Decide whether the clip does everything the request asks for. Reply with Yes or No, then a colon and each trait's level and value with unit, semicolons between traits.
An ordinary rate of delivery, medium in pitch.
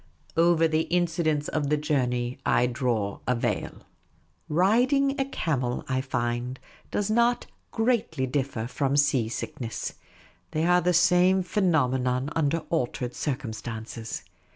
No: slow, 125 wpm; medium, 145 Hz